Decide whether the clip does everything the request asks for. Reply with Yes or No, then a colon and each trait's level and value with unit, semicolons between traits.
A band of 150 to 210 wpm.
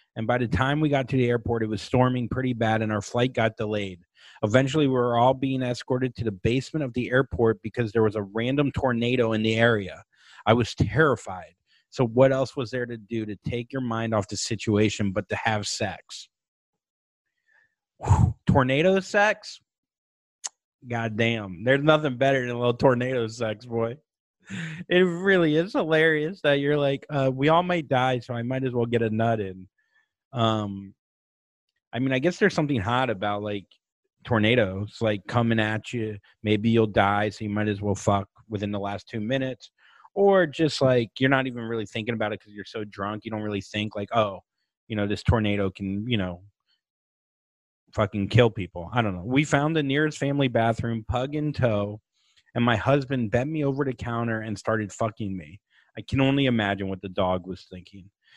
Yes: average, 190 wpm